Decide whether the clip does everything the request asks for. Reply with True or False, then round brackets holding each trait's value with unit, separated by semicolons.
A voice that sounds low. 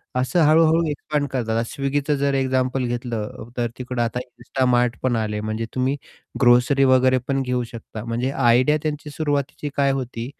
True (130 Hz)